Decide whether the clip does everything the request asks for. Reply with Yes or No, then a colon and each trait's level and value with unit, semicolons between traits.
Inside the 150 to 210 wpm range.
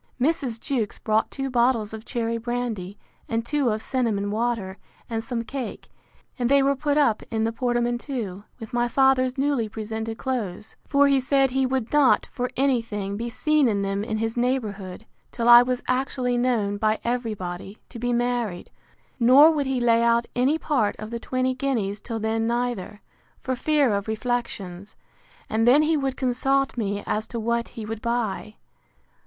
Yes: average, 180 wpm